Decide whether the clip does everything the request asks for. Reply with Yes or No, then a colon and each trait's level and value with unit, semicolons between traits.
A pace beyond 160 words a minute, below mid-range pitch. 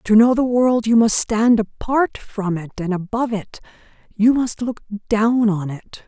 No: average, 190 wpm; high, 220 Hz